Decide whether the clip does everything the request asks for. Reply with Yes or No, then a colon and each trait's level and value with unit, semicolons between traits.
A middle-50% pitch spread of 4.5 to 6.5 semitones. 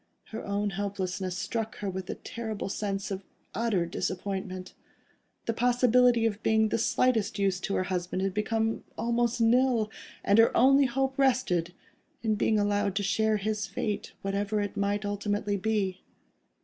No: narrow, 2.5 semitones